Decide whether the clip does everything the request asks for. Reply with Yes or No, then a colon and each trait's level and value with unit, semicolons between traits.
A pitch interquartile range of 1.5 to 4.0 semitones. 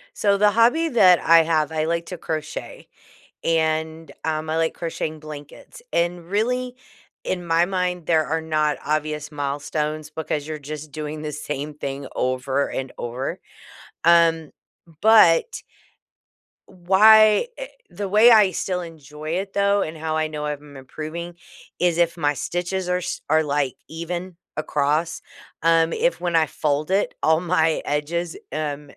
Yes: average, 2.9 semitones